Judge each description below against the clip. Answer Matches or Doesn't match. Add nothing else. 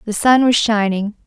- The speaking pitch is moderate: Doesn't match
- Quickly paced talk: Doesn't match